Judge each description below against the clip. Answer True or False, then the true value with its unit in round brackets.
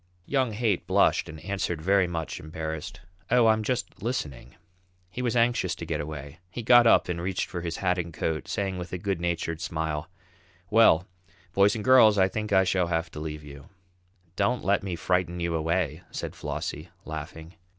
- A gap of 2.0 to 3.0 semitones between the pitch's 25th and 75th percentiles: False (4.2 semitones)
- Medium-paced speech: True (185 wpm)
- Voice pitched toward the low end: True (90 Hz)